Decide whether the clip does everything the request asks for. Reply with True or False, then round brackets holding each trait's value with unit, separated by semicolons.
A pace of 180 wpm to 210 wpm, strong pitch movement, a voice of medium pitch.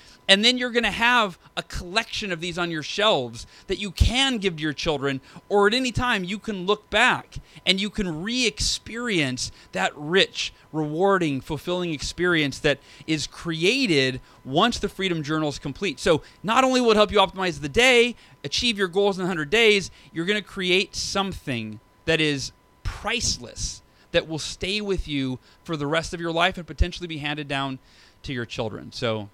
True (185 wpm; 6.1 semitones; 175 Hz)